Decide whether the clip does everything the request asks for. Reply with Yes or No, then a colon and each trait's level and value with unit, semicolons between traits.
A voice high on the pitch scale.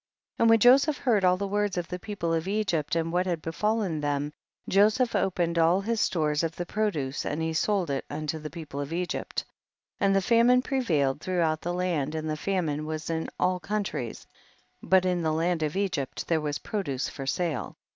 No: medium, 175 Hz